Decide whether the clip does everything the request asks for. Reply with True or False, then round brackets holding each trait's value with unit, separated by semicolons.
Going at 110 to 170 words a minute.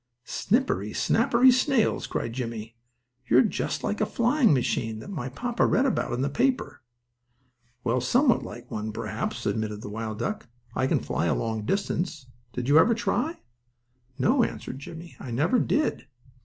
True (160 wpm)